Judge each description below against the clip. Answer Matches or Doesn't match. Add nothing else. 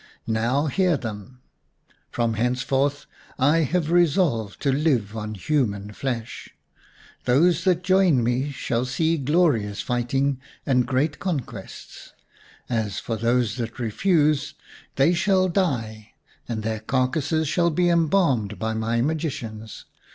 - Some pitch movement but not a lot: Doesn't match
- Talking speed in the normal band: Doesn't match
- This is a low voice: Matches